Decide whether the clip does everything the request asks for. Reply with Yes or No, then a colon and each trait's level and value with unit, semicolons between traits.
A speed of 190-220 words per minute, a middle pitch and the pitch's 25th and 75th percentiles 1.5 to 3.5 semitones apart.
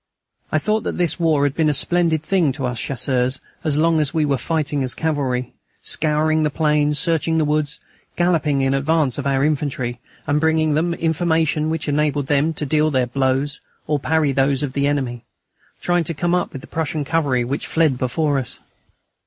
Yes: average, 195 wpm; medium, 150 Hz; average, 2.7 semitones